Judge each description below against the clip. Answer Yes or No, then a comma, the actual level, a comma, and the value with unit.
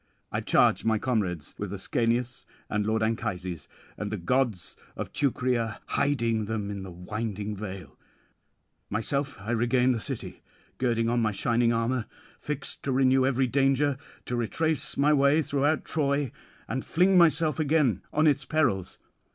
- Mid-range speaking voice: No, low, 120 Hz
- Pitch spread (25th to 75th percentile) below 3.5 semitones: No, average, 4.4 semitones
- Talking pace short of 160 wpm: Yes, average, 150 wpm